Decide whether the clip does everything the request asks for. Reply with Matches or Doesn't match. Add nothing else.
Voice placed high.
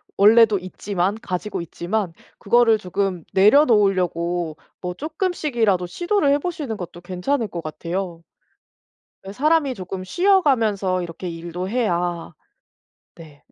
Matches